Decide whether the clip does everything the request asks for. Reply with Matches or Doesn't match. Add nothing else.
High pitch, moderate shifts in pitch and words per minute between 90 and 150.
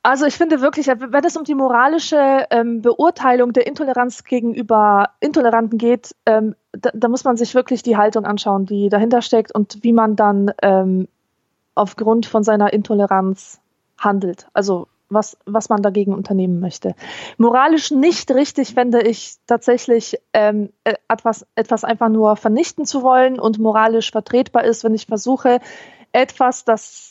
Matches